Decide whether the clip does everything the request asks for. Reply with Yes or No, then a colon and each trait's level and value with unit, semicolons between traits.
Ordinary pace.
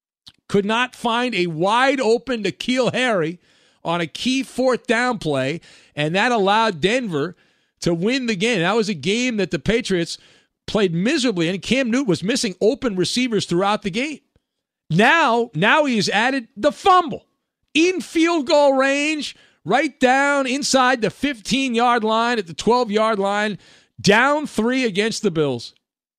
Yes: average, 160 wpm